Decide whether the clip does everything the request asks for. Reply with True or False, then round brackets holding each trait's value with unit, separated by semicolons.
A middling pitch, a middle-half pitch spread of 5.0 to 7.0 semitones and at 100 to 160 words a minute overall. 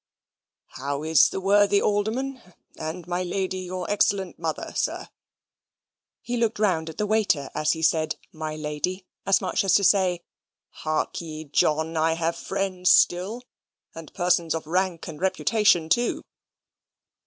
False (180 Hz; 3.7 semitones; 145 wpm)